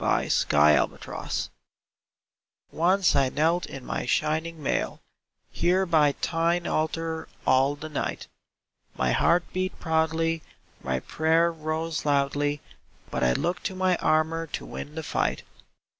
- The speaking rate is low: Yes, slow, 130 wpm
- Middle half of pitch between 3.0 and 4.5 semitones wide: No, narrow, 2.4 semitones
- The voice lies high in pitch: No, medium, 160 Hz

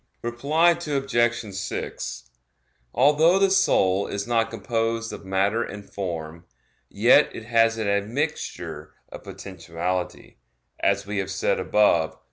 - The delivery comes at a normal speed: No, slow, 125 wpm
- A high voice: No, low, 110 Hz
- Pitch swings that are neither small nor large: Yes, average, 3.9 semitones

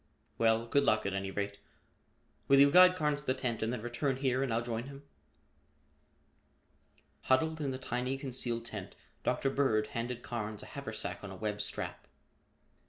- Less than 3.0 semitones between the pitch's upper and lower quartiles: No, average, 3.9 semitones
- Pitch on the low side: Yes, low, 120 Hz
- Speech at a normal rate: Yes, average, 170 wpm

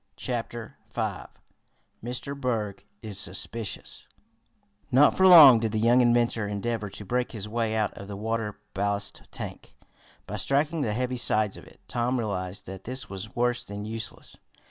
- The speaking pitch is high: No, low, 115 Hz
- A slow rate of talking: No, average, 160 wpm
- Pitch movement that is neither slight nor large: Yes, average, 3.2 semitones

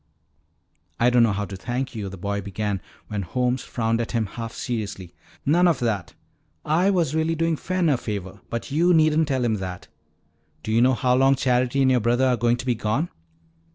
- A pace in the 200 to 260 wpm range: Yes, fast, 205 wpm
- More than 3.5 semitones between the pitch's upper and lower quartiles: Yes, average, 4.3 semitones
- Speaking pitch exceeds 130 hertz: No, low, 120 Hz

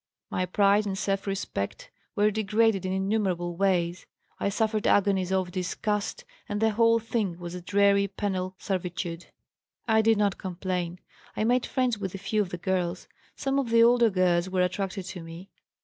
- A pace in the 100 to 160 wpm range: No, average, 175 wpm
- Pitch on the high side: Yes, high, 195 Hz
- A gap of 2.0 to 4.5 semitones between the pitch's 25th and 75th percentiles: Yes, narrow, 2.6 semitones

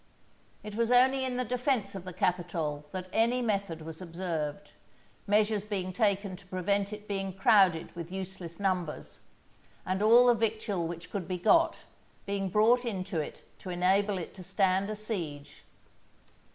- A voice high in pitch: Yes, high, 195 Hz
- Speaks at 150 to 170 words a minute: Yes, average, 160 wpm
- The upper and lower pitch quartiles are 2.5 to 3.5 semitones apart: Yes, average, 3.1 semitones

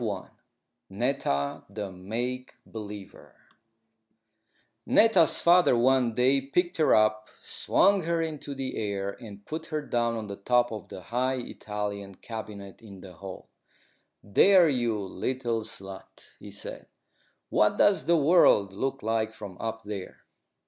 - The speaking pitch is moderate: No, low, 115 Hz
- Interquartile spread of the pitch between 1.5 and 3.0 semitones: No, average, 5.0 semitones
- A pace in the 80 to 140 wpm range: Yes, slow, 135 wpm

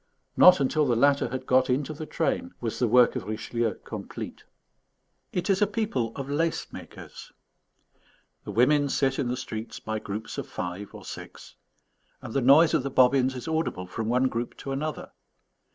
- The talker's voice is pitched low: Yes, low, 130 Hz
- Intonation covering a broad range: No, average, 4.2 semitones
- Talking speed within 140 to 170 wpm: No, average, 180 wpm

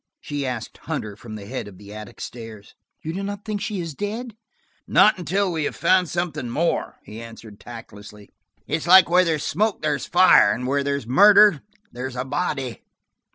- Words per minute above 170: Yes, average, 180 wpm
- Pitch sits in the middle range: Yes, medium, 145 Hz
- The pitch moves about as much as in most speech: No, wide, 8.0 semitones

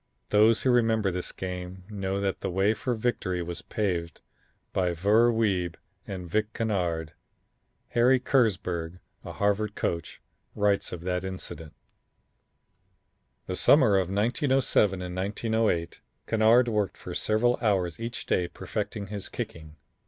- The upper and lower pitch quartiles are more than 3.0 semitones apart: Yes, average, 3.6 semitones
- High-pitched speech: No, low, 100 Hz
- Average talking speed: No, slow, 130 wpm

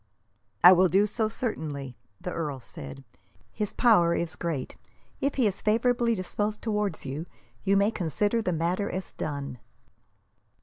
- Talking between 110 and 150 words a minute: Yes, average, 145 wpm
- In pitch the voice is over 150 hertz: Yes, medium, 185 Hz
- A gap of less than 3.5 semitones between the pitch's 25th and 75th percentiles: No, average, 5.1 semitones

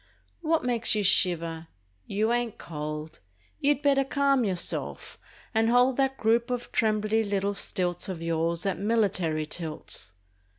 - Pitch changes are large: Yes, wide, 6.2 semitones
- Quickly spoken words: No, slow, 135 wpm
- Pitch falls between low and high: No, high, 210 Hz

